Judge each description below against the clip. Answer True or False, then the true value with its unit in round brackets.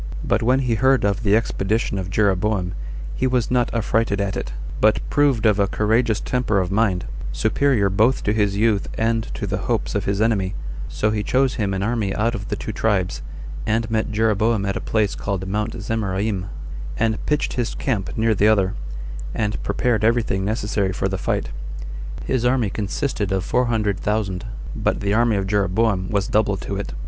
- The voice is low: True (105 Hz)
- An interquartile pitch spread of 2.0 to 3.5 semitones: True (2.6 semitones)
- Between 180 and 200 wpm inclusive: True (190 wpm)